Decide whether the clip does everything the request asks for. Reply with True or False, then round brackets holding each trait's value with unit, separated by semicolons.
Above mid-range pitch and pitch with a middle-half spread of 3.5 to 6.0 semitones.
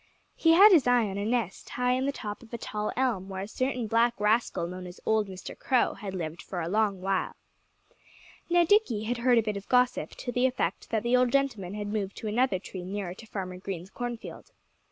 True (220 Hz; 4.4 semitones)